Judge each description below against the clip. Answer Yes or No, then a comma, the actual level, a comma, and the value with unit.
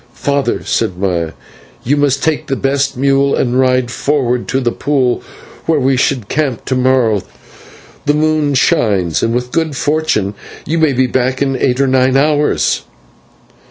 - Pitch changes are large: No, narrow, 2.6 semitones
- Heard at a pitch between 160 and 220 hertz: No, low, 130 Hz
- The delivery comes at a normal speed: Yes, average, 160 wpm